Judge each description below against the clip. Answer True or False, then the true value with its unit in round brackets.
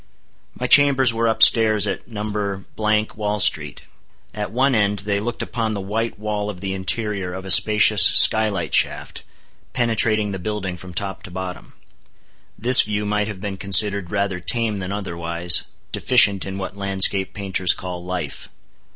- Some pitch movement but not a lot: False (2.2 semitones)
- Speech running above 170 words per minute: False (160 wpm)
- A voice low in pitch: True (100 Hz)